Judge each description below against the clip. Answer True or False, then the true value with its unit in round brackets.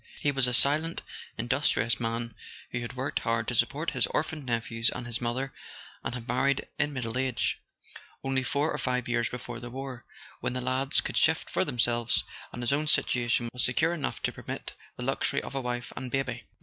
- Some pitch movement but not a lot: False (2.2 semitones)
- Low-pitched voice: True (125 Hz)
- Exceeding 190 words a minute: True (200 wpm)